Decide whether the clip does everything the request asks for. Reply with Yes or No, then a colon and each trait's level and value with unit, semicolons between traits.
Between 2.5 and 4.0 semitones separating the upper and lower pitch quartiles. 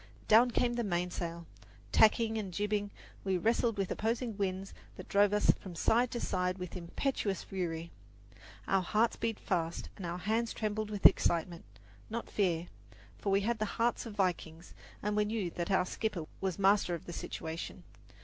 Yes: average, 3.5 semitones